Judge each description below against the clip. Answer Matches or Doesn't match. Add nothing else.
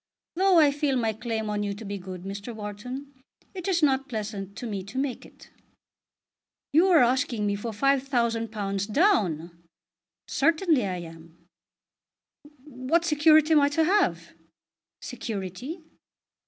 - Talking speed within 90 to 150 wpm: Matches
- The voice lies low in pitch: Doesn't match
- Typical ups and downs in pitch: Doesn't match